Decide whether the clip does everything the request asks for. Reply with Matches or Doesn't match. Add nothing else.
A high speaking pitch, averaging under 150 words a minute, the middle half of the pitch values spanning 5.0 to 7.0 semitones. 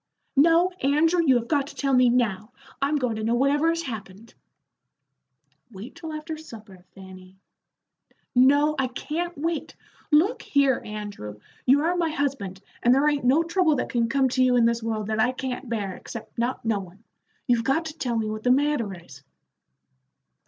Doesn't match